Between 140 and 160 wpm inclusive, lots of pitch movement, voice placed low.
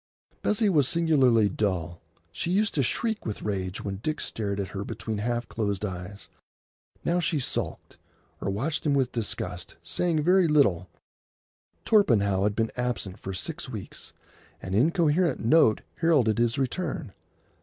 Yes: average, 145 wpm; wide, 8.1 semitones; low, 120 Hz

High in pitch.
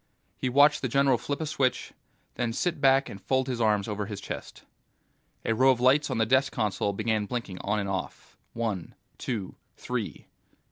No: low, 120 Hz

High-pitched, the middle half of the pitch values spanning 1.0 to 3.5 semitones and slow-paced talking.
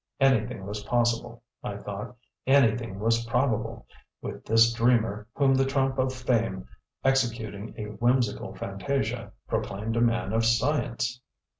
No: low, 115 Hz; average, 2.7 semitones; slow, 130 wpm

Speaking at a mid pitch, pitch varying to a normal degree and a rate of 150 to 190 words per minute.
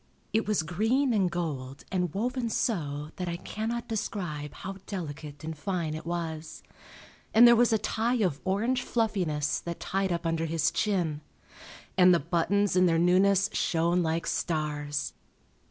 Yes: medium, 175 Hz; average, 4.6 semitones; average, 155 wpm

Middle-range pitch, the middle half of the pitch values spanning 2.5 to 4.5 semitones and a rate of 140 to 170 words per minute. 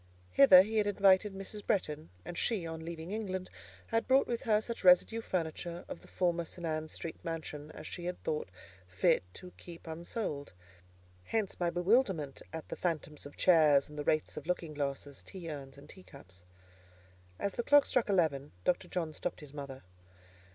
No: medium, 170 Hz; average, 4.1 semitones; average, 180 wpm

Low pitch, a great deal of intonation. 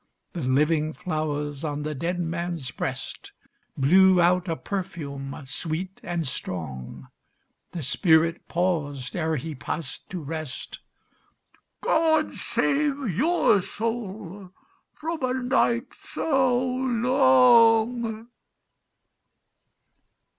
No: medium, 180 Hz; wide, 7.7 semitones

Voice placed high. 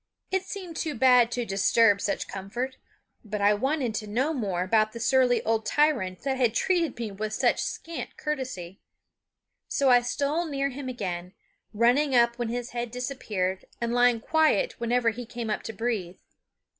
Yes: high, 240 Hz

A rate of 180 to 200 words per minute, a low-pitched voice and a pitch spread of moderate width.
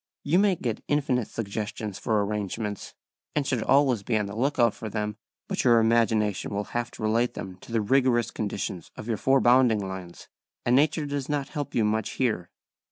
Yes: average, 195 wpm; low, 115 Hz; average, 3.8 semitones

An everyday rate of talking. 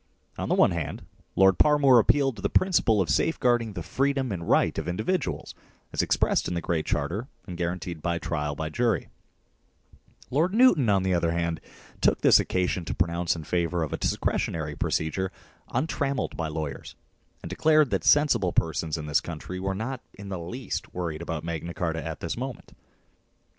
Yes: average, 180 wpm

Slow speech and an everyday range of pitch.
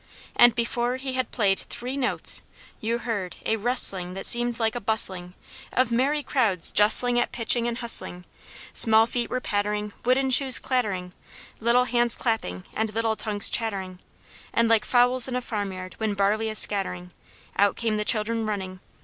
No: average, 165 wpm; average, 3.1 semitones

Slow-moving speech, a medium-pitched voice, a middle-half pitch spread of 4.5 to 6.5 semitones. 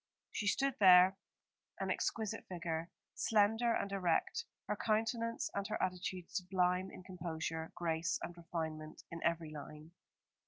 No: slow, 130 wpm; medium, 180 Hz; average, 3.8 semitones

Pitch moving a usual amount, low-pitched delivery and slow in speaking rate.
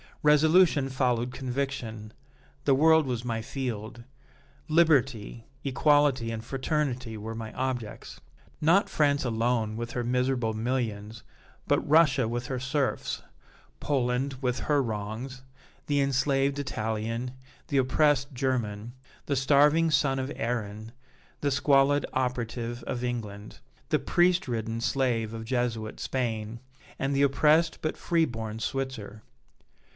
Yes: average, 3.6 semitones; low, 125 Hz; slow, 120 wpm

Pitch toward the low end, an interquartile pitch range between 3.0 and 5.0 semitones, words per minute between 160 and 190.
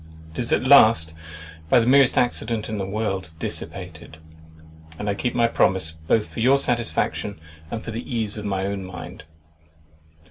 Yes: low, 110 Hz; average, 3.7 semitones; average, 170 wpm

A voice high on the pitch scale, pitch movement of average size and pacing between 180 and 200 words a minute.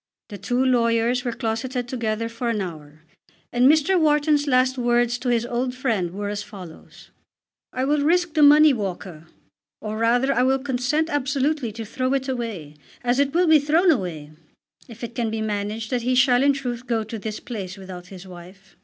Yes: high, 240 Hz; average, 4.1 semitones; average, 190 wpm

